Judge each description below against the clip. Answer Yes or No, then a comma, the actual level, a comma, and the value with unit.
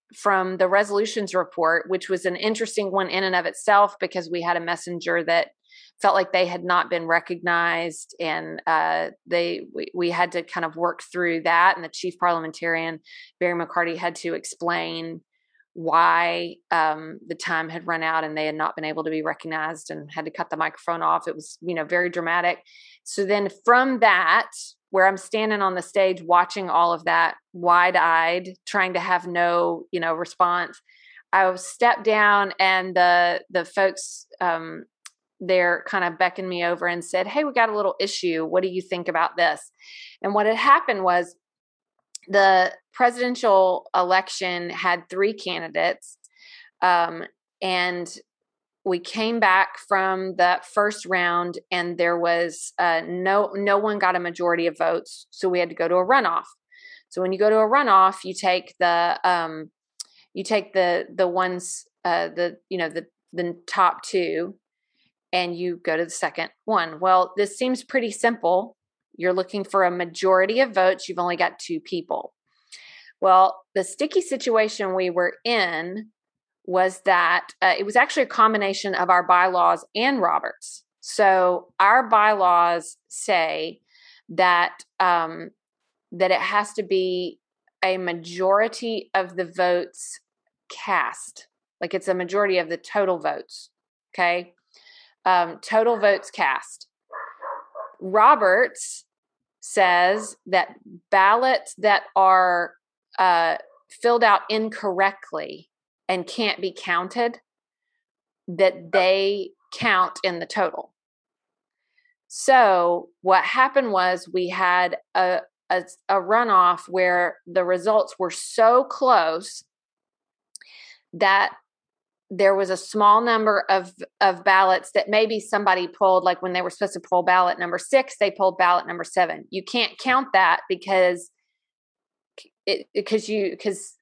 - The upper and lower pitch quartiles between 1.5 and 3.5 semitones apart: Yes, average, 2.9 semitones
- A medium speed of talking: Yes, average, 150 wpm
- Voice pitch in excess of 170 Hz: Yes, medium, 185 Hz